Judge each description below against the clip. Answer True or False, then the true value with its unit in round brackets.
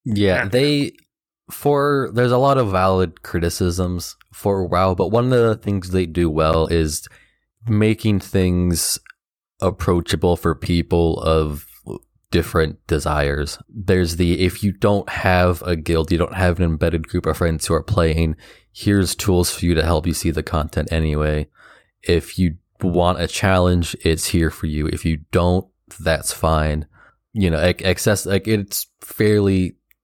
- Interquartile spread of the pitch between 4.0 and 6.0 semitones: False (3.4 semitones)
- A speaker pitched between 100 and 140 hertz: False (90 Hz)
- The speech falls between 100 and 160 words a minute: True (155 wpm)